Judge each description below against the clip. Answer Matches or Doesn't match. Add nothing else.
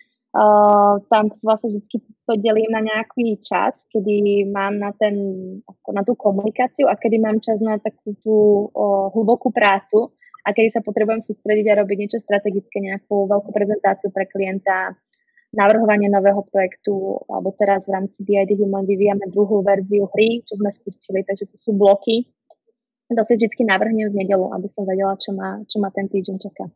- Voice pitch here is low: Doesn't match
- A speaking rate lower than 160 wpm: Doesn't match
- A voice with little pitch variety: Matches